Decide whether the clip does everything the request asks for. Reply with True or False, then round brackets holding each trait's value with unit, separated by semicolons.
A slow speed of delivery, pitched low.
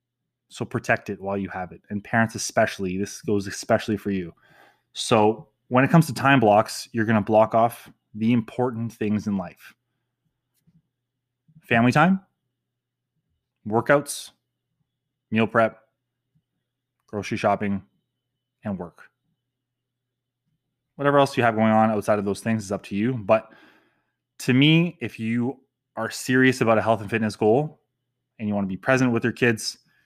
False (155 wpm; 120 Hz)